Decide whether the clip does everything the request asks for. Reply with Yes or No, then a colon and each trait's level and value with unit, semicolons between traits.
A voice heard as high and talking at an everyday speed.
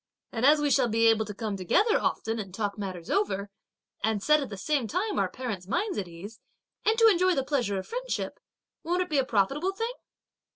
No: high, 245 Hz; fast, 215 wpm